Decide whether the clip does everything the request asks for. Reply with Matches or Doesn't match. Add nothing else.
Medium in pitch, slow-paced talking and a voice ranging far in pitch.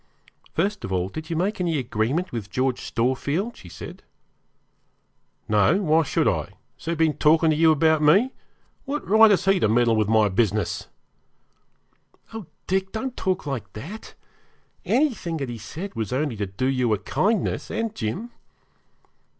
Doesn't match